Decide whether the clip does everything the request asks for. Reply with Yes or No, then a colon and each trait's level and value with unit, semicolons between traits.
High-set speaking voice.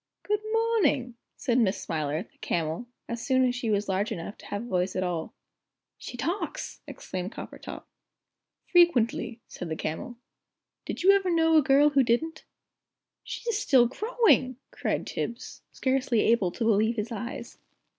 Yes: high, 240 Hz